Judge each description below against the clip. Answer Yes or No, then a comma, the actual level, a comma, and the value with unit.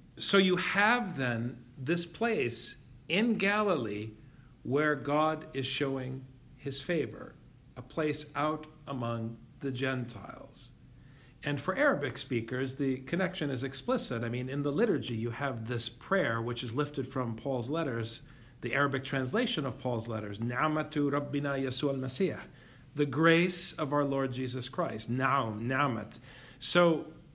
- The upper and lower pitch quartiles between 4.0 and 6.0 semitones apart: No, average, 3.6 semitones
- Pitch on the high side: No, low, 135 Hz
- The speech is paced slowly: Yes, slow, 130 wpm